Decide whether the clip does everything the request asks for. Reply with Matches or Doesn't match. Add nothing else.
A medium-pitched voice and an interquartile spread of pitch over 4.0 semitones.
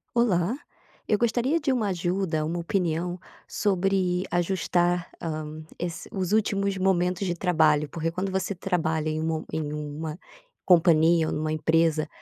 Doesn't match